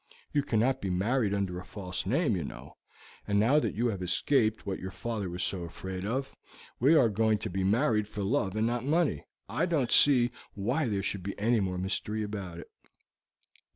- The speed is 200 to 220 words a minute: Yes, fast, 205 wpm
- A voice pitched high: No, low, 105 Hz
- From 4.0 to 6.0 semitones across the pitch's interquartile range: Yes, average, 4.3 semitones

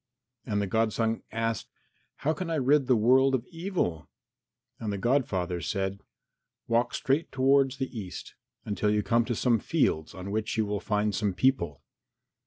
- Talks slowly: No, average, 165 wpm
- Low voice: Yes, low, 115 Hz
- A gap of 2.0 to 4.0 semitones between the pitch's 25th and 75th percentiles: No, average, 4.6 semitones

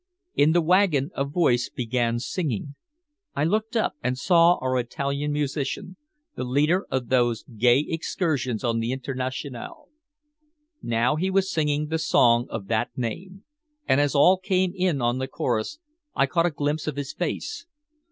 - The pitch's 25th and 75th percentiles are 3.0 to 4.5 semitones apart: No, wide, 5.4 semitones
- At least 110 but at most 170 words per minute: Yes, average, 160 wpm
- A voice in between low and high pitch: Yes, medium, 145 Hz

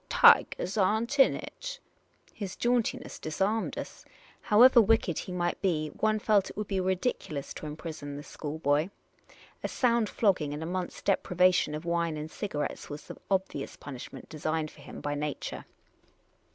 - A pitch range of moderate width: No, wide, 5.8 semitones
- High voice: No, medium, 180 Hz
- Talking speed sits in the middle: Yes, average, 160 wpm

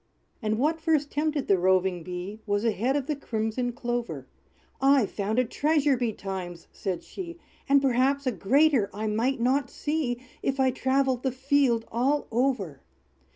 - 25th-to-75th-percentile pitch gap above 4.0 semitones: Yes, average, 4.4 semitones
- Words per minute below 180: Yes, average, 160 wpm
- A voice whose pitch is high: Yes, very high, 250 Hz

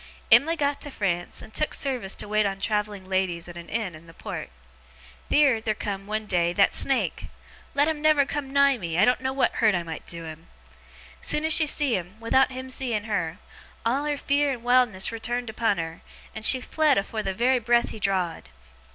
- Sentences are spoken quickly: Yes, fast, 210 wpm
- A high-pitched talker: Yes, high, 220 Hz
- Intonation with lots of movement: Yes, wide, 5.8 semitones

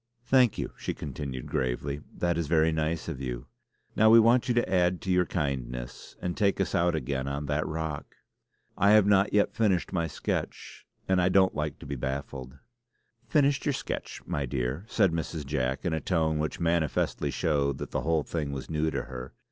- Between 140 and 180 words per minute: No, average, 195 wpm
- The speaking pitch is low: Yes, very low, 80 Hz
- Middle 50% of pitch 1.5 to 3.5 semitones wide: No, average, 5.0 semitones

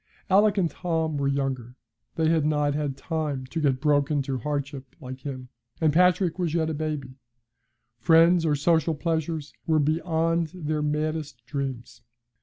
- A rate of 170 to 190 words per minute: No, average, 155 wpm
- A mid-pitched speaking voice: Yes, medium, 150 Hz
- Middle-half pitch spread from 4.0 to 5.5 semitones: No, average, 2.8 semitones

